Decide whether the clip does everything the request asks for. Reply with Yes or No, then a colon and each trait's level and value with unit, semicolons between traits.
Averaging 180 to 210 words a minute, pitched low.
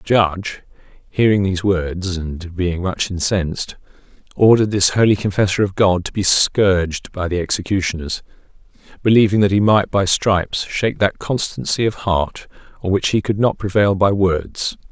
No: average, 160 wpm; very low, 95 Hz